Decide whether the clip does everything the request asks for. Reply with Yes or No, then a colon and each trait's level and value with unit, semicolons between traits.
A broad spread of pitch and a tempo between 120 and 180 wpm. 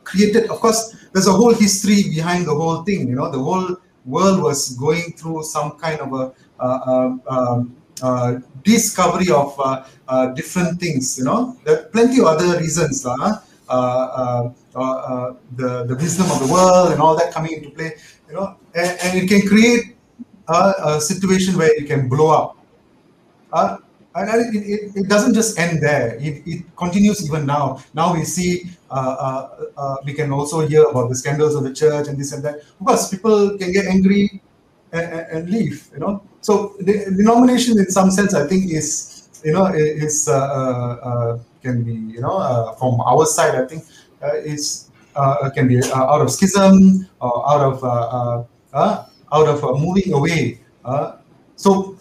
No: wide, 6.3 semitones; average, 190 wpm